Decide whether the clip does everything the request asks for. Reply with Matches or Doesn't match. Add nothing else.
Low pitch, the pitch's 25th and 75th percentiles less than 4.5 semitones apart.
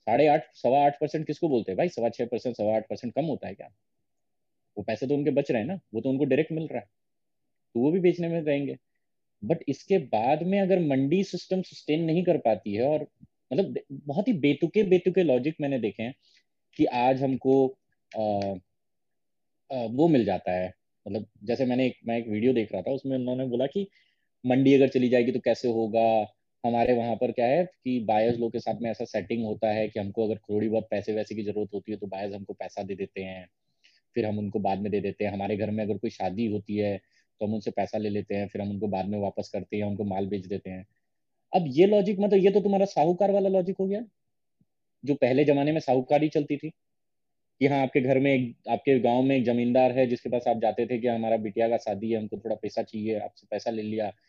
Doesn't match